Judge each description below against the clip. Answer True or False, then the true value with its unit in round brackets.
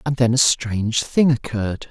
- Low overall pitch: True (120 Hz)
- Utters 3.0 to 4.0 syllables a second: False (5.0 syllables/s)